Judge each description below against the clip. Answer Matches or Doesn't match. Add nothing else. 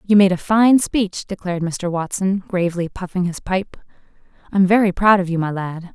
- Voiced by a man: Doesn't match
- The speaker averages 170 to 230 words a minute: Matches